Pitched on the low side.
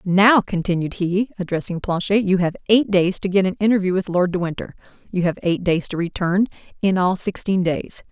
No: medium, 185 Hz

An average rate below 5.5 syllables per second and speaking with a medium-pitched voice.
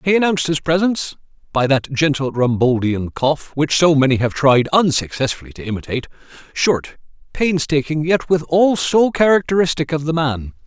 Yes: 5.0 syllables/s; medium, 150 Hz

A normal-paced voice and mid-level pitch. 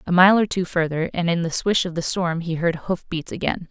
No: fast, 260 wpm; medium, 170 Hz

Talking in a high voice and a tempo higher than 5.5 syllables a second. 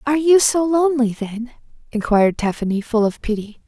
Yes: high, 245 Hz; 5.8 syllables/s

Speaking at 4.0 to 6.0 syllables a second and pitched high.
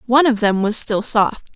Yes: 5.1 syllables/s; high, 225 Hz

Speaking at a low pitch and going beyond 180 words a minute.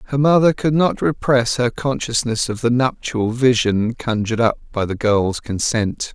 No: low, 120 Hz; average, 165 wpm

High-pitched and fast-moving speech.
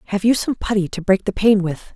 Yes: high, 205 Hz; fast, 275 wpm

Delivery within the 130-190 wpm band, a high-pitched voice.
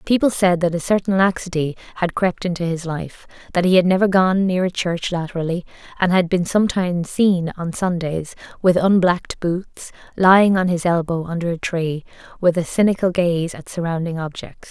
No: average, 180 wpm; medium, 175 Hz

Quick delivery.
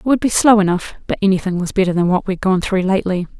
Yes: fast, 265 wpm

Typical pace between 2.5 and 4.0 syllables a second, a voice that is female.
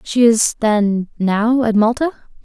Yes: 3.7 syllables/s; female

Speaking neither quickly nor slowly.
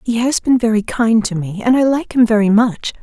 No: fast, 260 wpm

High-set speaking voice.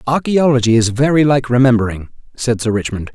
No: low, 125 Hz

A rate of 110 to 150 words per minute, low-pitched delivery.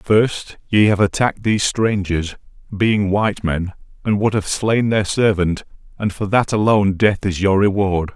No: average, 170 wpm; low, 100 Hz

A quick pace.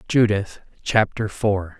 No: slow, 100 wpm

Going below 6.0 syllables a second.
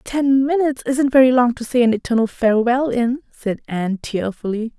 Yes: 5.4 syllables/s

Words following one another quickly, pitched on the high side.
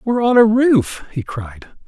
No: average, 190 wpm; high, 200 Hz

